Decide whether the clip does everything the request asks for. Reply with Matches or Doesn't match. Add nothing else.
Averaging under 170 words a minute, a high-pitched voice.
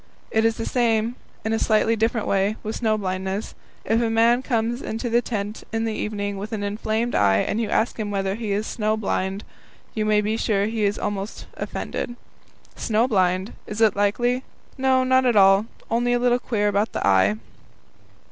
Doesn't match